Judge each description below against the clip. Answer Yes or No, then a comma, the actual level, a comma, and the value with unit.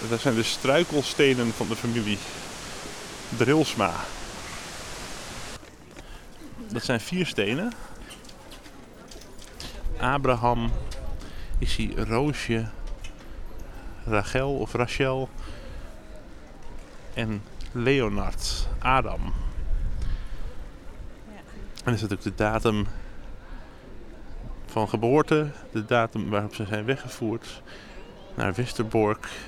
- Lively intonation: No, average, 3.6 semitones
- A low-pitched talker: Yes, low, 115 Hz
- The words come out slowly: Yes, slow, 75 wpm